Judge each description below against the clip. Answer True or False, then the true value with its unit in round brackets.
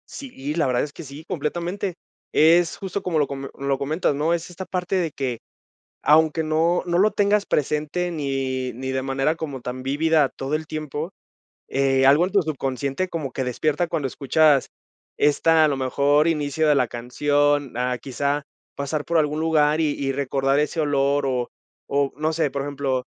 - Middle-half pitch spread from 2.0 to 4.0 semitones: True (2.9 semitones)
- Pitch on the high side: False (145 Hz)